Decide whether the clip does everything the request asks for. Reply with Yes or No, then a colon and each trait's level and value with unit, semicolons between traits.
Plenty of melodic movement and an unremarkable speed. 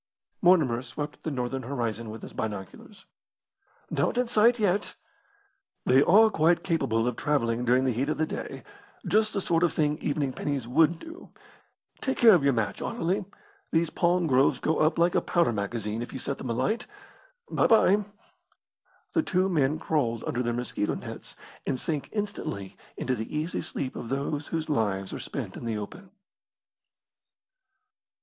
Yes: wide, 6.6 semitones; average, 170 wpm